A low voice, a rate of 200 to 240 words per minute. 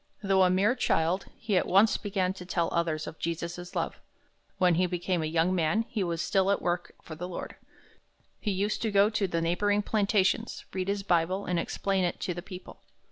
No: medium, 185 Hz; fast, 205 wpm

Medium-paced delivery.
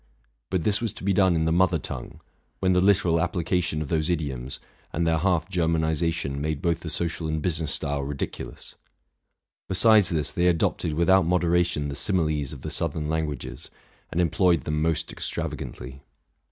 Yes: average, 175 wpm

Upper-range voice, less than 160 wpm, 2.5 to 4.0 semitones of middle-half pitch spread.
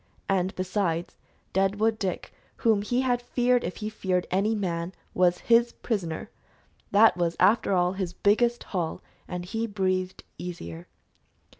Yes: high, 195 Hz; average, 140 wpm; average, 3.7 semitones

